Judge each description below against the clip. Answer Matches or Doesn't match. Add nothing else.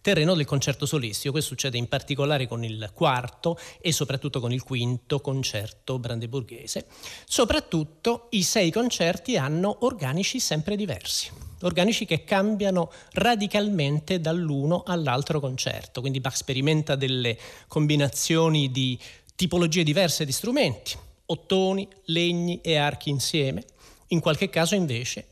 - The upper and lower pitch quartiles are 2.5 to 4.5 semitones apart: Doesn't match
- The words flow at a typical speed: Matches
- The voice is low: Doesn't match